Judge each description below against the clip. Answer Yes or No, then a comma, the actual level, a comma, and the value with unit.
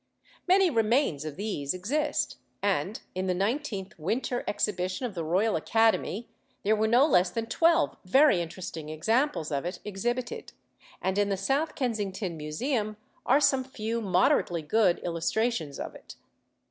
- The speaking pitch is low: No, high, 205 Hz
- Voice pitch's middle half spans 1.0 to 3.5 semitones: No, wide, 5.4 semitones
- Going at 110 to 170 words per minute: Yes, average, 145 wpm